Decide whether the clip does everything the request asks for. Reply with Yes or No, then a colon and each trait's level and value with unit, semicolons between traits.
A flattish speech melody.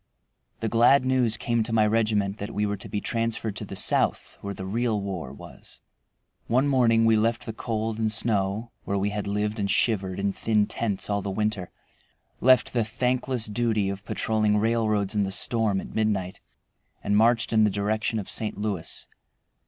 Yes: narrow, 2.0 semitones